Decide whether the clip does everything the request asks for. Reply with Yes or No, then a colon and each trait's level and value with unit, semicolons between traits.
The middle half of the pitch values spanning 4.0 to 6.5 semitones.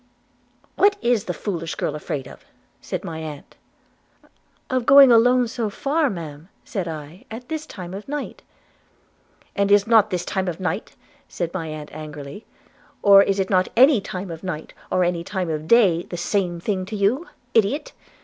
Yes: wide, 5.4 semitones